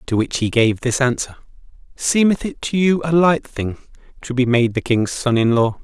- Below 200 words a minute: No, fast, 205 wpm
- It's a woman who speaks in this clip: No, male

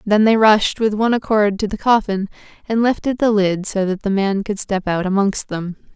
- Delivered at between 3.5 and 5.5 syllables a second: Yes, 5.1 syllables/s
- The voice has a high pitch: Yes, high, 205 Hz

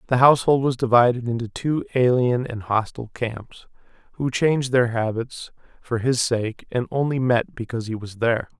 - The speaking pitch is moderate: No, low, 120 Hz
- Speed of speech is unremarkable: Yes, average, 170 wpm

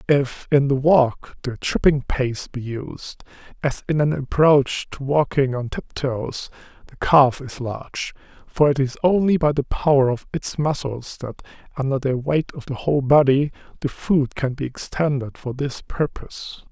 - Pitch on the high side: No, low, 135 Hz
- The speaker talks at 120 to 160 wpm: No, average, 170 wpm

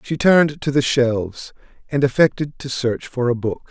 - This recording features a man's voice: Yes, male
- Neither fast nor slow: Yes, average, 195 wpm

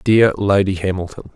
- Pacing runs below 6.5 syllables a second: Yes, 5.0 syllables/s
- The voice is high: No, very low, 95 Hz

